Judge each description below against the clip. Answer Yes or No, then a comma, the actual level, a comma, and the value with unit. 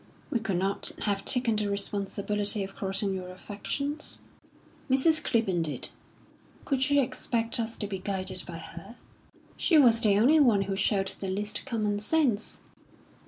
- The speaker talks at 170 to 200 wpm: No, average, 155 wpm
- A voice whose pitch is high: Yes, high, 210 Hz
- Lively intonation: No, average, 3.7 semitones